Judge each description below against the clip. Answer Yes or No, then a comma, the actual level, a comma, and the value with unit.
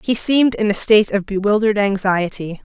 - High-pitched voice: Yes, high, 205 Hz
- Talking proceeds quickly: No, average, 175 wpm